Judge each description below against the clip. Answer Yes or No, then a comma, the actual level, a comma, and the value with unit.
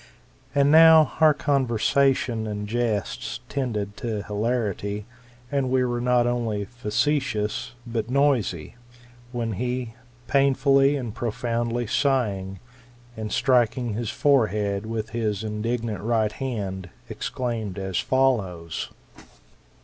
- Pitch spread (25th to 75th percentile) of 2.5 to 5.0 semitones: Yes, average, 3.5 semitones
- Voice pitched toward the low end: Yes, low, 115 Hz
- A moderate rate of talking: No, slow, 105 wpm